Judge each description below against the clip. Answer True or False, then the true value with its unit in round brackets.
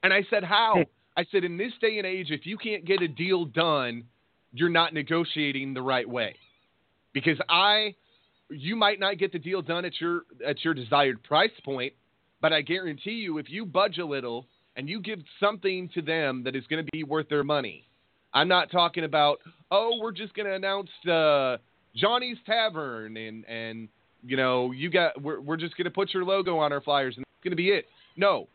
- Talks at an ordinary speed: False (210 wpm)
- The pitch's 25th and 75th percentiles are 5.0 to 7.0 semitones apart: True (5.4 semitones)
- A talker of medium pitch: True (165 Hz)